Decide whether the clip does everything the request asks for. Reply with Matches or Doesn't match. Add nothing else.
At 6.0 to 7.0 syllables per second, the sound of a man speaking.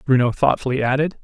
Matches